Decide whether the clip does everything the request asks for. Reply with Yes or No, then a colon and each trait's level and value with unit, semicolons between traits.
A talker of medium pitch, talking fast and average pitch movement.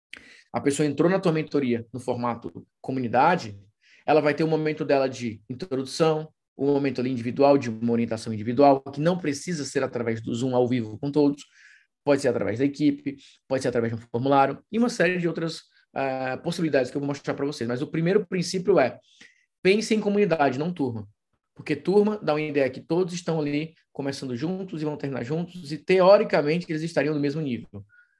Yes: medium, 145 Hz; fast, 195 wpm; average, 4.0 semitones